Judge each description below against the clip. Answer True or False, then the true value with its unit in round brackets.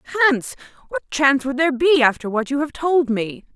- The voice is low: False (275 Hz)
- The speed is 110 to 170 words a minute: False (205 wpm)